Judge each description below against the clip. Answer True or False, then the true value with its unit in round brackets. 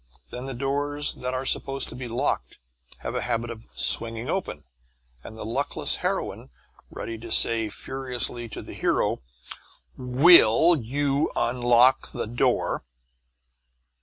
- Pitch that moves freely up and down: False (3.0 semitones)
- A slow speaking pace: True (130 wpm)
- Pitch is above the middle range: False (125 Hz)